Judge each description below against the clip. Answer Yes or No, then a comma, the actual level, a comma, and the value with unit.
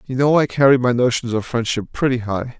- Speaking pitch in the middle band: No, low, 125 Hz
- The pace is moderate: No, fast, 230 wpm